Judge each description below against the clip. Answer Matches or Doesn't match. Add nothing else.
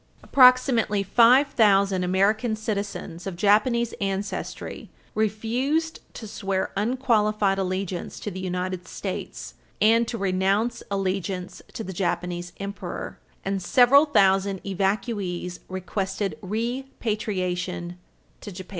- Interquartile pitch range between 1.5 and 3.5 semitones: Matches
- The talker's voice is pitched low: Doesn't match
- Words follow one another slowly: Matches